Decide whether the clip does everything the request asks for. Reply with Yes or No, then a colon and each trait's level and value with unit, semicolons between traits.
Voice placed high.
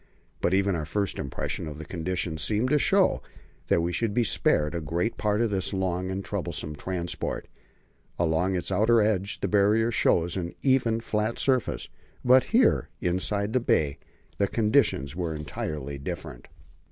No: very low, 95 Hz